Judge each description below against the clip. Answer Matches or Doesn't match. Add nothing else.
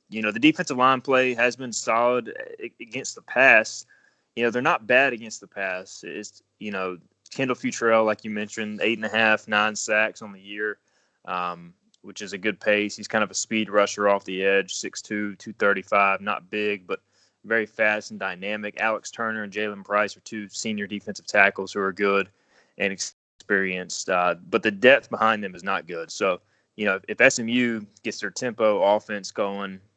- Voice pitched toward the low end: Matches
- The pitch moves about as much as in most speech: Doesn't match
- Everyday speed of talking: Matches